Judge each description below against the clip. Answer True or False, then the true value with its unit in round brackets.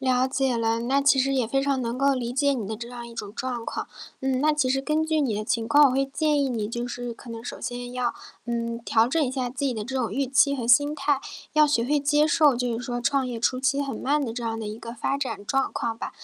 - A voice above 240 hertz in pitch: True (255 Hz)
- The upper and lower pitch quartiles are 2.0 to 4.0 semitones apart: True (2.8 semitones)